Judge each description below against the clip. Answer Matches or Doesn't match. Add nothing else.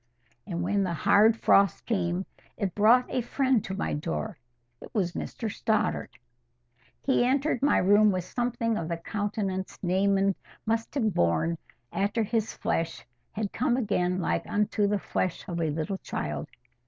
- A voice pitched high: Matches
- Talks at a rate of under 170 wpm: Matches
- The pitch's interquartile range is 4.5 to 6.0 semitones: Doesn't match